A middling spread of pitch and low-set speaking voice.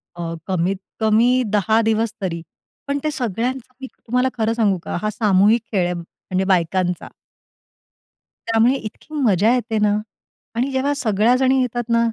No: average, 4.5 semitones; high, 225 Hz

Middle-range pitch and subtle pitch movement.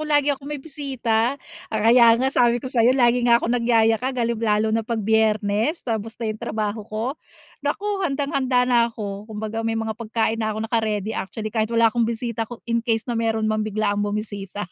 No: high, 225 Hz; narrow, 2.0 semitones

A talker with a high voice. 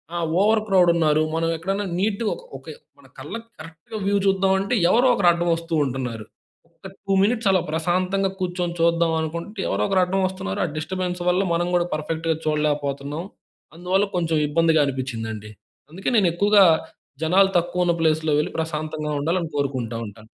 No: medium, 170 Hz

